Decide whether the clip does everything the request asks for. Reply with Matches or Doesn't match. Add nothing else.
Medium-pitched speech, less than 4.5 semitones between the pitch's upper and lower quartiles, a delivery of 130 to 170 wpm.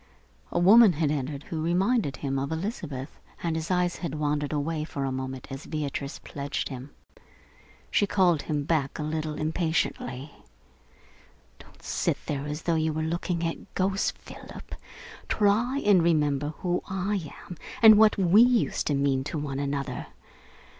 Matches